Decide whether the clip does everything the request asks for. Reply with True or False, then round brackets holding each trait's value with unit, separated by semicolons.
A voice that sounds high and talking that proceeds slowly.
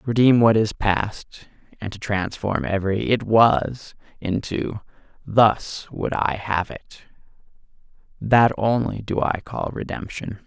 False (105 Hz; 125 wpm)